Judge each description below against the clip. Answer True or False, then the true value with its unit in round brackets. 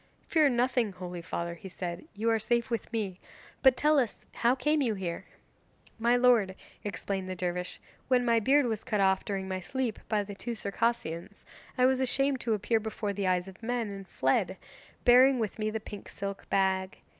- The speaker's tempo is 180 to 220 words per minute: True (190 wpm)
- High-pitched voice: True (215 Hz)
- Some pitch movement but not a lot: True (4.4 semitones)